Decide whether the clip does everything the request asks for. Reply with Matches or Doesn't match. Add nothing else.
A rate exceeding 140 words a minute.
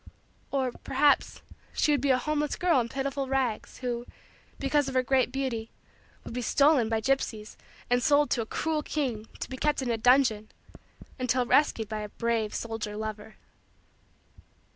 Matches